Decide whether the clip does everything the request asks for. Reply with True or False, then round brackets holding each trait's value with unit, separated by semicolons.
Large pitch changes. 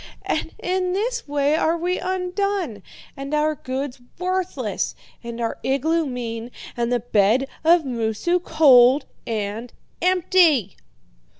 True (6.9 semitones)